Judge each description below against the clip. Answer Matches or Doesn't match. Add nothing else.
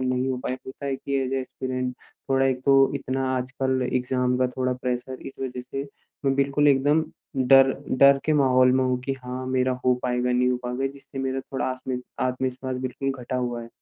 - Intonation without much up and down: Matches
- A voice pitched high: Doesn't match